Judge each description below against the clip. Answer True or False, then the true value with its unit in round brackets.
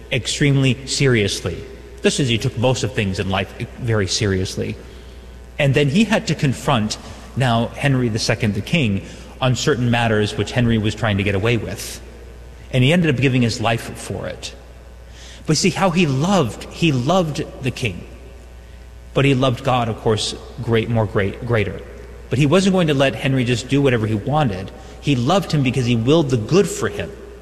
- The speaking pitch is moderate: False (120 Hz)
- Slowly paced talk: False (185 wpm)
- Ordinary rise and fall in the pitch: False (5.8 semitones)